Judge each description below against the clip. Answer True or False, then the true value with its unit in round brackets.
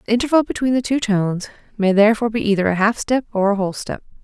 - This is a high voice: True (215 Hz)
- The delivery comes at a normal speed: False (240 wpm)